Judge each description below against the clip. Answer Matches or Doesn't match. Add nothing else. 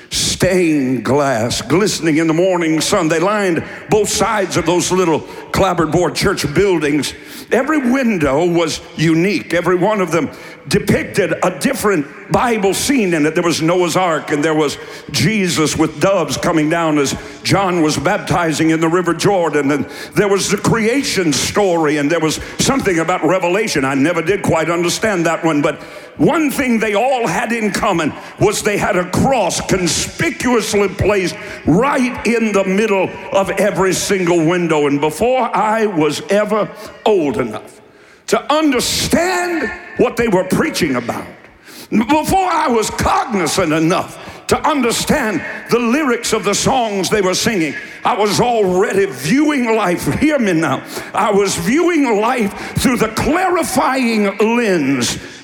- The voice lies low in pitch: Doesn't match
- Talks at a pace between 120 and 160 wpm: Matches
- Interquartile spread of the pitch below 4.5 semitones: Doesn't match